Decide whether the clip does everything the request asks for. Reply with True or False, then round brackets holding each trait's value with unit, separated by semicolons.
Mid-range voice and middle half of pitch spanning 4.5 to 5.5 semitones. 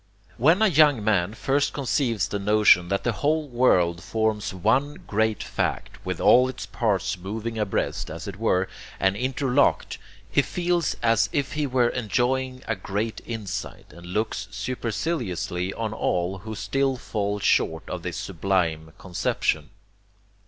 False (110 Hz; 5.0 semitones)